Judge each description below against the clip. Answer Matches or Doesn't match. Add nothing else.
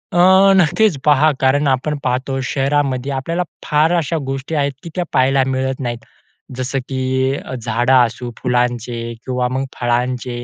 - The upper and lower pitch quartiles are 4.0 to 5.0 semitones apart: Doesn't match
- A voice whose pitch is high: Doesn't match